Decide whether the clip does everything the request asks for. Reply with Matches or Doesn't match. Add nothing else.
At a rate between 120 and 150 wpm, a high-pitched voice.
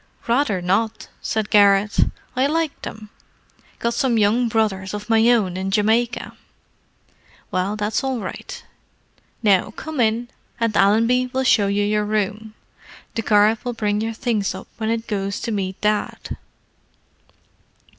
Matches